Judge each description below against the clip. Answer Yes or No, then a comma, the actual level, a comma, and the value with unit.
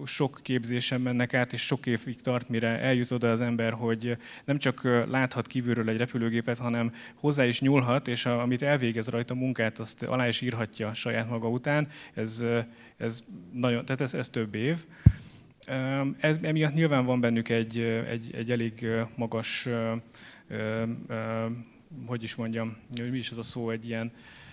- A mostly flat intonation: Yes, narrow, 2.0 semitones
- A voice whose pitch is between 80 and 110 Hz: No, low, 120 Hz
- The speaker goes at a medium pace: No, fast, 160 wpm